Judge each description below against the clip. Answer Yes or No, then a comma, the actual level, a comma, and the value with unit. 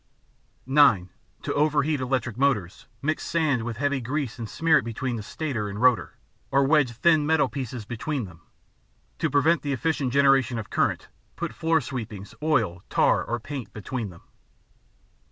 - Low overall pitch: Yes, low, 130 Hz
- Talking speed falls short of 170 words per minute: Yes, average, 160 wpm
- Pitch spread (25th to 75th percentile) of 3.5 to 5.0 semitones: Yes, average, 4.5 semitones